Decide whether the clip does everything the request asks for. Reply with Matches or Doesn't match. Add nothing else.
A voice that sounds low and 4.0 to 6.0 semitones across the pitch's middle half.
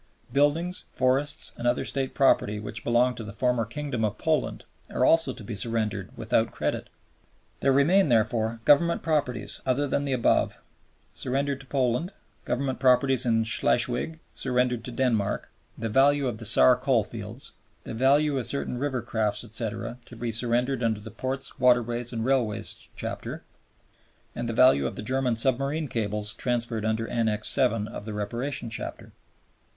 Doesn't match